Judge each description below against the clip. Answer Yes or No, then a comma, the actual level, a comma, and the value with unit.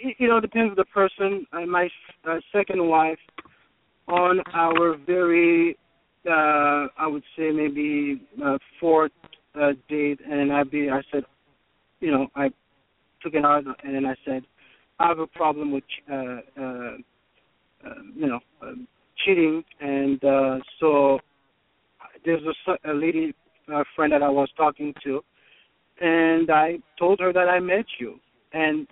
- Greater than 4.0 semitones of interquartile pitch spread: No, average, 3.6 semitones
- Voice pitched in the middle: Yes, medium, 155 Hz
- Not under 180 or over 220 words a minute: No, average, 155 wpm